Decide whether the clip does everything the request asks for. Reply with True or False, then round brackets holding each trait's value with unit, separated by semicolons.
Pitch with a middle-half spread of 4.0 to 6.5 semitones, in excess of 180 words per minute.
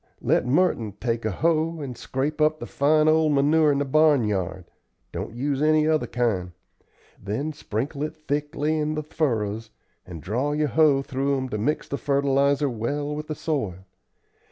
False (4.5 semitones; 170 wpm)